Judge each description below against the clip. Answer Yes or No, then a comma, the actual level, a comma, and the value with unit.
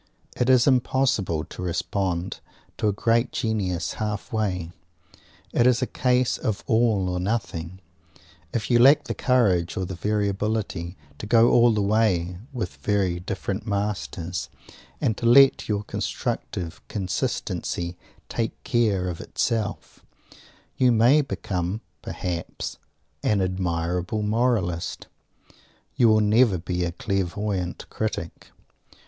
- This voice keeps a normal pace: No, slow, 120 wpm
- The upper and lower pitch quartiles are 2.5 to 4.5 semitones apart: Yes, average, 4.2 semitones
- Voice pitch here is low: Yes, low, 100 Hz